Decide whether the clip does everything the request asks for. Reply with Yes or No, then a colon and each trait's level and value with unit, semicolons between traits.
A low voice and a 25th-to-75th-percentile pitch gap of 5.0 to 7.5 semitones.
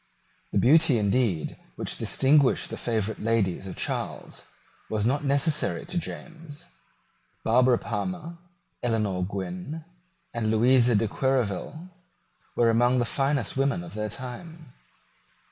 Yes: low, 125 Hz; wide, 5.5 semitones